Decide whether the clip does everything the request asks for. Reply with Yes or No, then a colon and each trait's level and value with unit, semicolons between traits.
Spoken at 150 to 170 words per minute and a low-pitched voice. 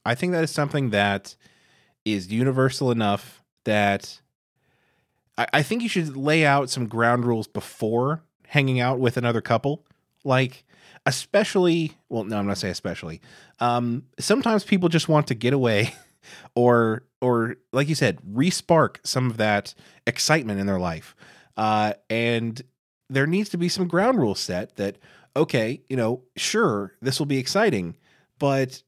Yes: average, 155 wpm; low, 130 Hz